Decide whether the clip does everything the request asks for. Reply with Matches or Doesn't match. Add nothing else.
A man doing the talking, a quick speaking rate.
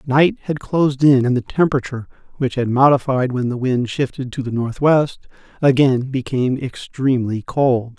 Doesn't match